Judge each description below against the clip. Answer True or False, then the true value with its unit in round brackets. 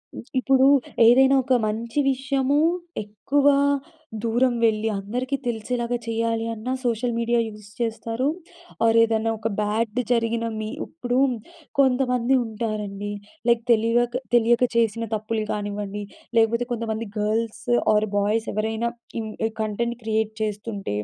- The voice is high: True (230 Hz)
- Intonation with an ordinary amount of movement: False (2.0 semitones)